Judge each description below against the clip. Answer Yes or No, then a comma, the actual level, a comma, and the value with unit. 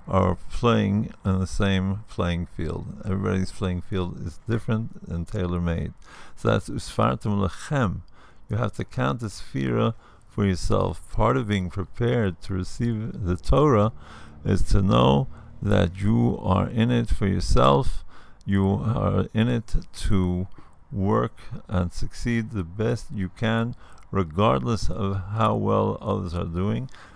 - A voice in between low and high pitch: No, low, 100 Hz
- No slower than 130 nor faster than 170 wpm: Yes, average, 140 wpm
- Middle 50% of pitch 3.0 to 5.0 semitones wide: Yes, average, 3.9 semitones